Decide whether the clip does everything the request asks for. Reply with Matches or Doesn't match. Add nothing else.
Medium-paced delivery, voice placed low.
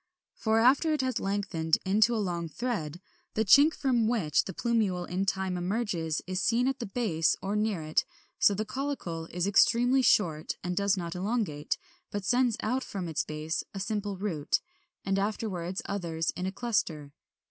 Doesn't match